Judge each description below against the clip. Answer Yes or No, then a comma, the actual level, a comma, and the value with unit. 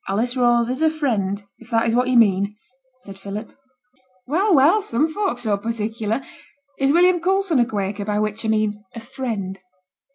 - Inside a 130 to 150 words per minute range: No, average, 175 wpm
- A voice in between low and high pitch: No, high, 230 Hz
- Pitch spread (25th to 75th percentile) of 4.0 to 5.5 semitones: Yes, average, 4.6 semitones